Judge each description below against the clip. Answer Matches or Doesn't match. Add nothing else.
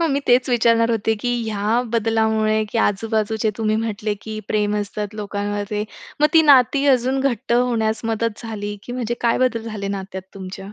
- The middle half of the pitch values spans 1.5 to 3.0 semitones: Matches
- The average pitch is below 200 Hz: Doesn't match